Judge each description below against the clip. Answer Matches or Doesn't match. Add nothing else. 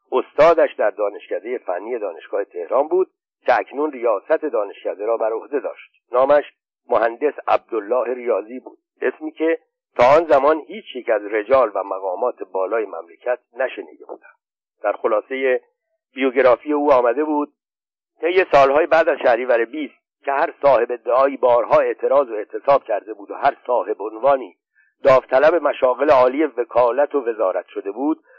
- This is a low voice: Doesn't match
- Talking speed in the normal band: Matches